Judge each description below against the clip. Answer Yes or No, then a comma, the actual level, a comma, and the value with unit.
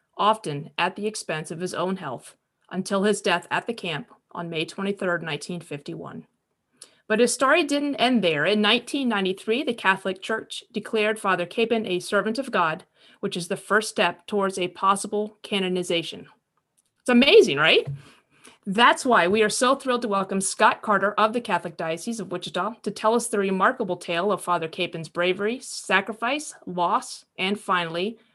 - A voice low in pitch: No, high, 200 Hz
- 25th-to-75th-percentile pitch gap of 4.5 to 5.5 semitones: No, average, 3.7 semitones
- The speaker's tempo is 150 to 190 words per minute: Yes, average, 165 wpm